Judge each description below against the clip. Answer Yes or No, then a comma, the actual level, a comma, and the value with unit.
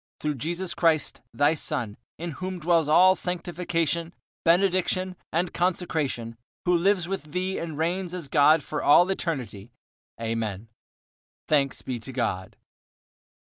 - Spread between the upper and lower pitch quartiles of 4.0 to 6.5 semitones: Yes, average, 4.3 semitones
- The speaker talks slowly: Yes, slow, 130 wpm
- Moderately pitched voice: Yes, medium, 165 Hz